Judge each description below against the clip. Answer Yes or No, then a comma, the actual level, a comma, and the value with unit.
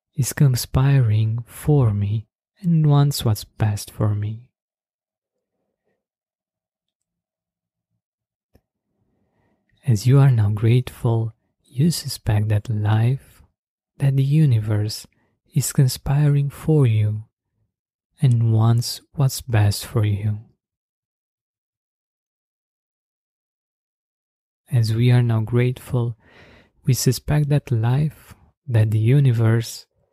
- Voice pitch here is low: Yes, low, 115 Hz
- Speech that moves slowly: Yes, slow, 90 wpm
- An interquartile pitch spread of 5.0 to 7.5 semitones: No, average, 3.9 semitones